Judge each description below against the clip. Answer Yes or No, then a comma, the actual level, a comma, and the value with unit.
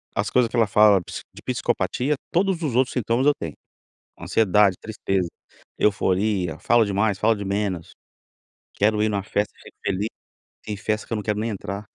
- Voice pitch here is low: Yes, low, 105 Hz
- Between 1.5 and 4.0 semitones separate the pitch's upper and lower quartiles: Yes, narrow, 2.4 semitones